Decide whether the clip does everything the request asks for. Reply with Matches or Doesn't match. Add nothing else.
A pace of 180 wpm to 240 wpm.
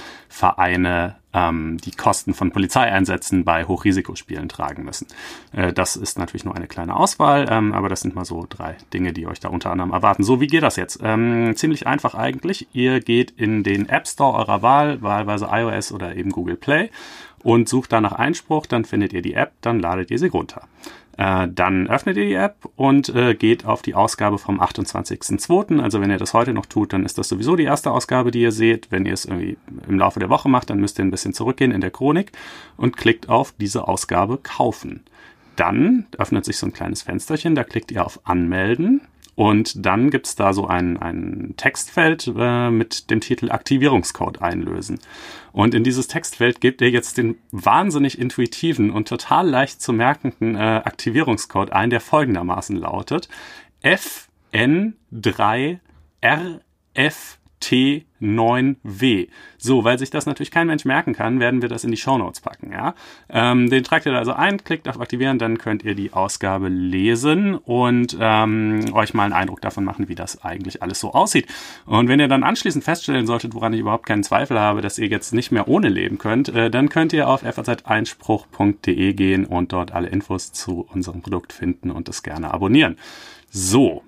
Matches